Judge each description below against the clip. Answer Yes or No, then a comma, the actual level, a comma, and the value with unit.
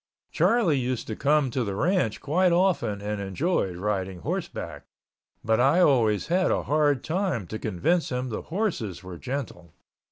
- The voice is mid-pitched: No, low, 125 Hz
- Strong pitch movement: Yes, wide, 8.2 semitones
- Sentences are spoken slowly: No, average, 160 wpm